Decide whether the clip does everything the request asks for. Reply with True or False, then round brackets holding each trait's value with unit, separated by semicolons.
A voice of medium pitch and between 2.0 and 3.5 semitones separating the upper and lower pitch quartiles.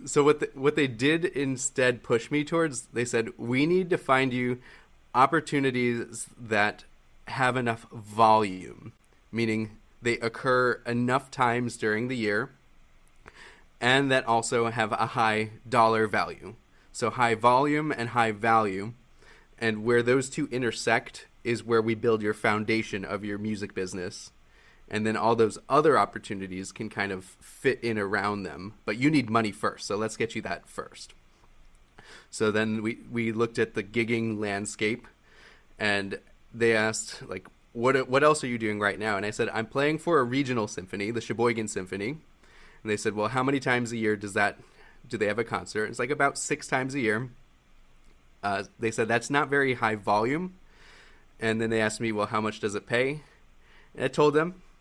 False (115 Hz; 3.1 semitones)